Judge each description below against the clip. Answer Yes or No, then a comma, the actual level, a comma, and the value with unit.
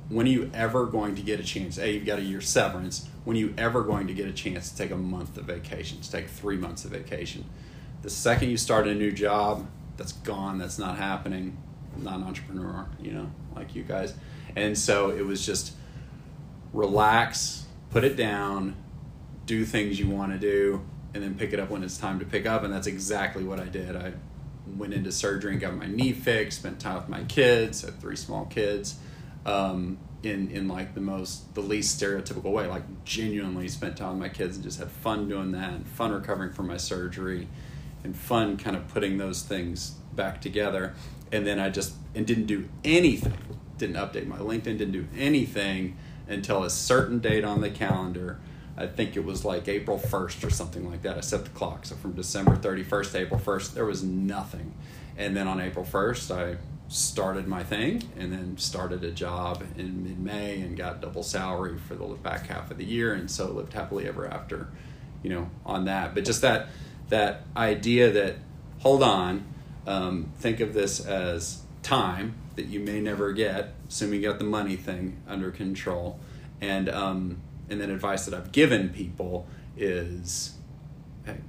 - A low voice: Yes, low, 100 Hz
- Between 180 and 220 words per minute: Yes, average, 200 wpm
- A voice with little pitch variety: Yes, narrow, 2.3 semitones